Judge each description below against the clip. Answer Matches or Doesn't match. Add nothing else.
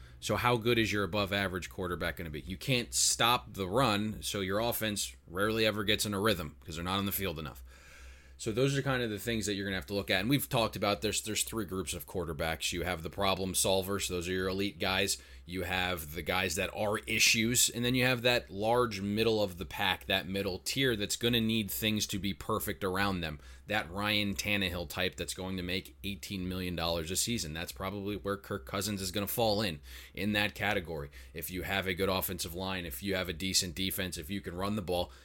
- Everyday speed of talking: Doesn't match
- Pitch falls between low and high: Doesn't match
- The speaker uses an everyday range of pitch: Matches